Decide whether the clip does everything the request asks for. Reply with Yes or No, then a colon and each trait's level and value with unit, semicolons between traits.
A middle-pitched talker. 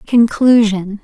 No: high, 220 Hz